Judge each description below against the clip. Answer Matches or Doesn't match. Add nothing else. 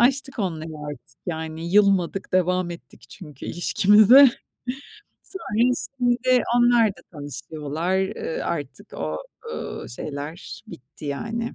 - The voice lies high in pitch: Doesn't match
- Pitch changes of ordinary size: Doesn't match